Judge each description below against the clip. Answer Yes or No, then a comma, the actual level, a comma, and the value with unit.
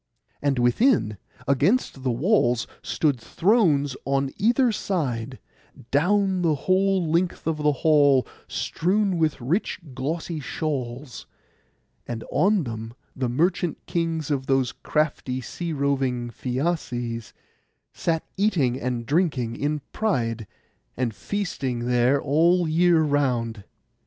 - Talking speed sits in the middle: No, slow, 115 wpm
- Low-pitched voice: No, medium, 145 Hz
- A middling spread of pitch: No, wide, 5.7 semitones